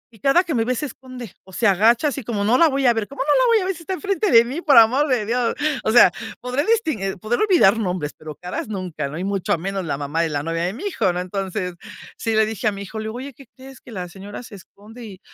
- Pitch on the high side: Yes, high, 220 Hz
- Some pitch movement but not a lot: No, wide, 5.8 semitones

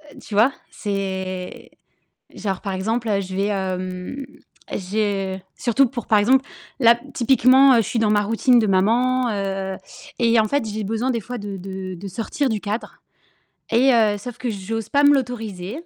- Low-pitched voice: No, high, 215 Hz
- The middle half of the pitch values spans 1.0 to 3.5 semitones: No, average, 3.9 semitones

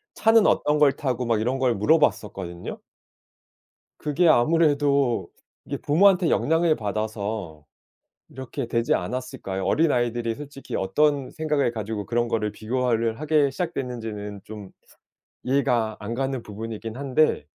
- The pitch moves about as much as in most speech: Yes, average, 5.0 semitones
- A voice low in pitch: Yes, low, 125 Hz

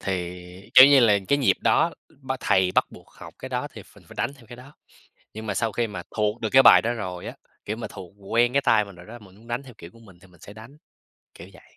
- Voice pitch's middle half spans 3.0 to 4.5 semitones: Yes, average, 4.2 semitones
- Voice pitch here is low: Yes, low, 110 Hz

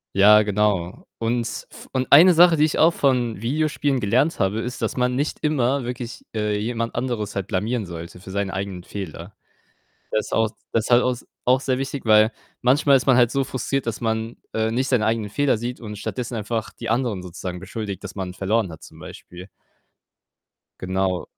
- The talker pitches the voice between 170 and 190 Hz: No, low, 115 Hz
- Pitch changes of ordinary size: Yes, average, 4.1 semitones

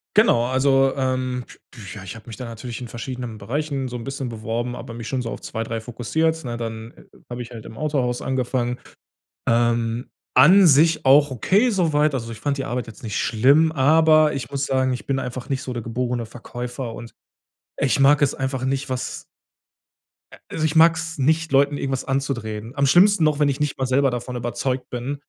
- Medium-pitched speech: No, low, 130 Hz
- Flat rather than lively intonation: No, average, 3.1 semitones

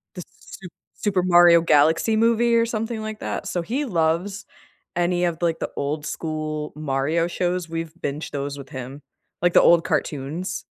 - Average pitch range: Yes, average, 3.7 semitones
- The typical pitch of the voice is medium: Yes, medium, 170 Hz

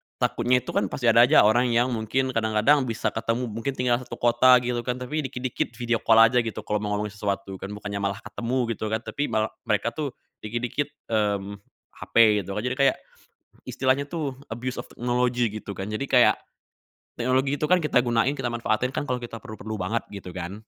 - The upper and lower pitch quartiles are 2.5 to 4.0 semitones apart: Yes, average, 2.9 semitones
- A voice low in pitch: Yes, low, 120 Hz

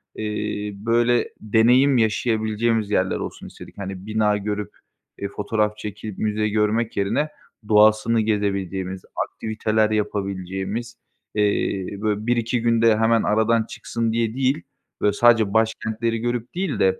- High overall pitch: No, low, 110 Hz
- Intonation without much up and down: Yes, narrow, 1.8 semitones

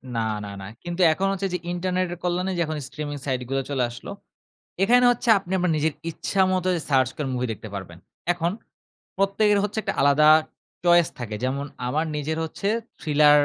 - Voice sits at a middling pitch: Yes, medium, 160 Hz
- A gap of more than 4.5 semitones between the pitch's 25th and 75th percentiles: Yes, average, 5.0 semitones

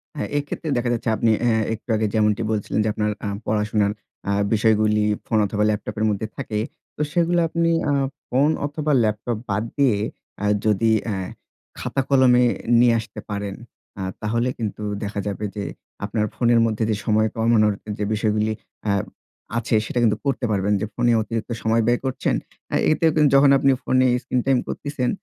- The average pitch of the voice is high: No, low, 110 Hz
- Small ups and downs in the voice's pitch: No, average, 3.1 semitones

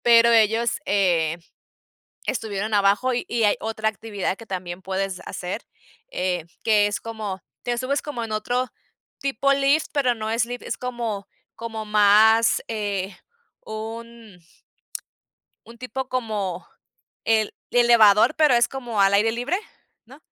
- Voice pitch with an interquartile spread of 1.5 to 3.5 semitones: Yes, average, 2.8 semitones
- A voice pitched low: No, high, 220 Hz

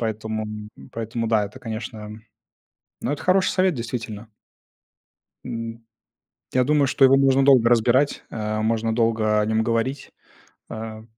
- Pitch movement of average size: Yes, average, 3.0 semitones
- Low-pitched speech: Yes, low, 115 Hz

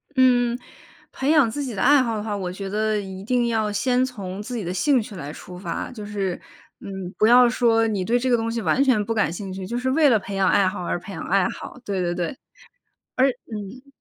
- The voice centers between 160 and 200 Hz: No, high, 215 Hz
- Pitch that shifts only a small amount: No, average, 4.2 semitones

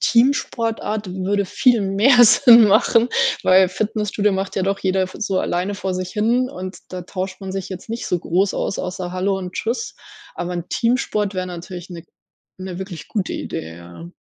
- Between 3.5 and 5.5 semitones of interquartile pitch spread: No, average, 2.8 semitones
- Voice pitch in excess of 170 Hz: Yes, high, 190 Hz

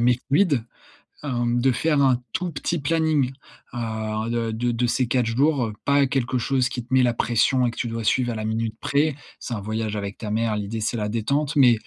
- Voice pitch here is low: Yes, low, 120 Hz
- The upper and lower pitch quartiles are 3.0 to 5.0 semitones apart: Yes, average, 3.3 semitones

